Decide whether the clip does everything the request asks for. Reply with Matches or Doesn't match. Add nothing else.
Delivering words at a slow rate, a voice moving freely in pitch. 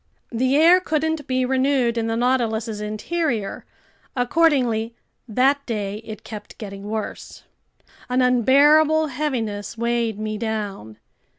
Doesn't match